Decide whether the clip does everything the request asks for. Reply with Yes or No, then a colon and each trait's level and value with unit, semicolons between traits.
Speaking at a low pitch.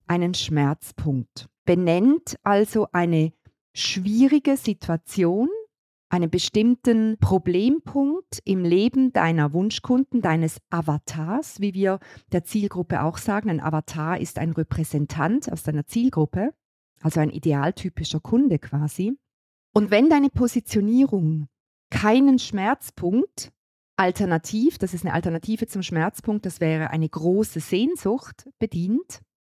No: medium, 185 Hz